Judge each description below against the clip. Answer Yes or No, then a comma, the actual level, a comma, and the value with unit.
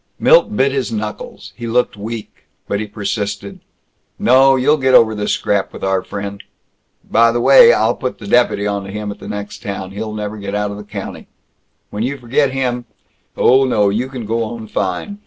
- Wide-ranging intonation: No, average, 3.8 semitones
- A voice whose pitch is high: No, low, 110 Hz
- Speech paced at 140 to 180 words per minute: No, average, 195 wpm